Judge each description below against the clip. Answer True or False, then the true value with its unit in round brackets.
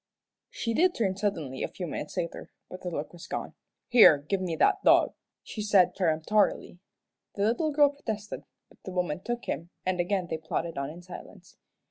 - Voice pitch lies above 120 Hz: True (185 Hz)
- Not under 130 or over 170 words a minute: False (185 wpm)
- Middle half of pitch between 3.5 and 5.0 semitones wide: True (4.3 semitones)